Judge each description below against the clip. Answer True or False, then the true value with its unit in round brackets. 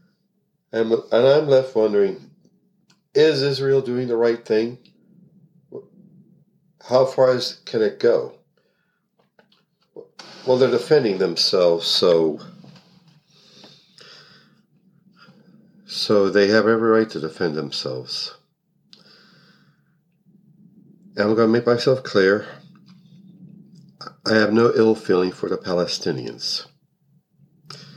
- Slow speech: True (95 wpm)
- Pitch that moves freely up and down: True (7.3 semitones)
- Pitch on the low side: False (175 Hz)